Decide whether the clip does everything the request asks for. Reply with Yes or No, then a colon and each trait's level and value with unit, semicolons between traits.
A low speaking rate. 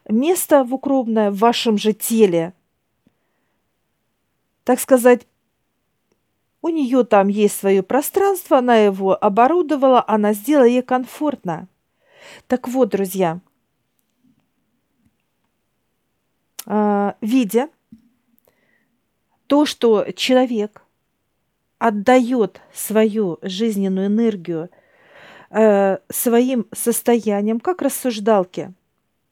Yes: slow, 75 wpm